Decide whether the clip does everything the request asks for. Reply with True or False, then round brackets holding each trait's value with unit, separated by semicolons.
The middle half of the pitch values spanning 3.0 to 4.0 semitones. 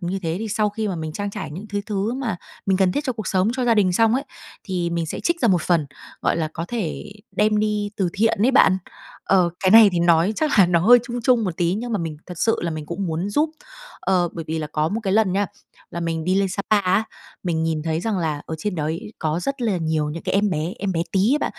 False (4.4 semitones)